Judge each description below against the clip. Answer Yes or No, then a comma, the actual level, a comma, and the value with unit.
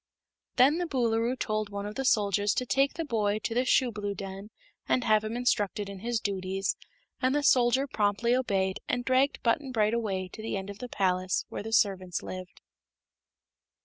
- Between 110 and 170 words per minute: No, average, 185 wpm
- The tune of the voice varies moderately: Yes, average, 3.8 semitones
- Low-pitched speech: No, high, 215 Hz